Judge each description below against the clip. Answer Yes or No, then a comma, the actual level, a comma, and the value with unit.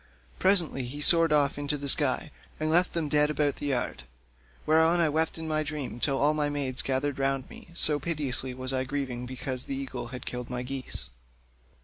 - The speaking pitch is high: No, medium, 145 Hz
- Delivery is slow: No, fast, 205 wpm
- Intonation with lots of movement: No, average, 2.9 semitones